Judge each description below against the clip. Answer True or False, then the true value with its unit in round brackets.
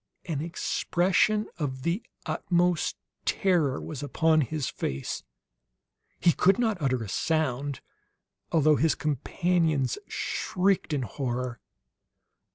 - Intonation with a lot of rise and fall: False (4.8 semitones)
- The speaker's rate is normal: False (105 wpm)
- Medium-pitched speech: True (155 Hz)